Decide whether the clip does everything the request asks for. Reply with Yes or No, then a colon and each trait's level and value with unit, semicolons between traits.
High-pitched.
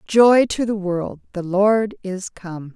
Yes: high, 200 Hz